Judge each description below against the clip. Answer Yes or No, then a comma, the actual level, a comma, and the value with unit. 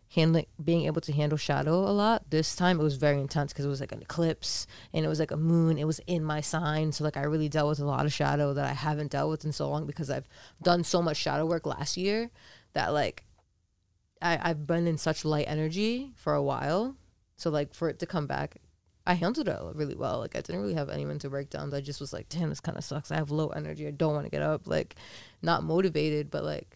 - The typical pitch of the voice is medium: Yes, medium, 150 Hz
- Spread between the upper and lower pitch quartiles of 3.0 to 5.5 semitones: No, narrow, 2.5 semitones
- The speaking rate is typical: No, fast, 255 wpm